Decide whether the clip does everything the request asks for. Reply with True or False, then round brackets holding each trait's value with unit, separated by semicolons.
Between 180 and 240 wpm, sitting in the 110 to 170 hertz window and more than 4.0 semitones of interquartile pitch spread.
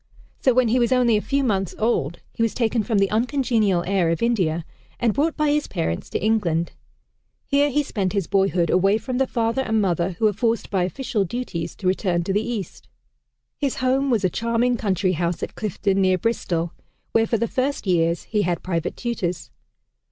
False (200 wpm; 215 Hz; 4.8 semitones)